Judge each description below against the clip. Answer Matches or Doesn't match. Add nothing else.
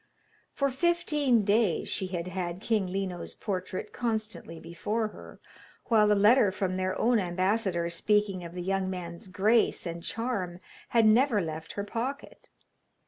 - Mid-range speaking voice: Doesn't match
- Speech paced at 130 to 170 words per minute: Matches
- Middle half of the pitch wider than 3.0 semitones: Matches